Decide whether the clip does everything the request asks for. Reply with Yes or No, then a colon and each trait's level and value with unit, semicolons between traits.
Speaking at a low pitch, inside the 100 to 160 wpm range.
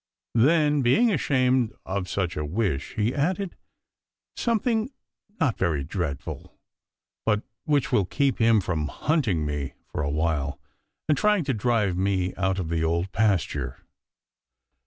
Yes: low, 105 Hz; slow, 135 wpm